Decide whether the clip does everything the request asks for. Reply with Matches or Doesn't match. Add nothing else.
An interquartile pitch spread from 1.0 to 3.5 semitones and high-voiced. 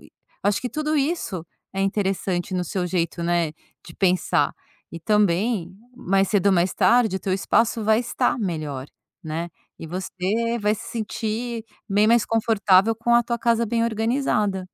Doesn't match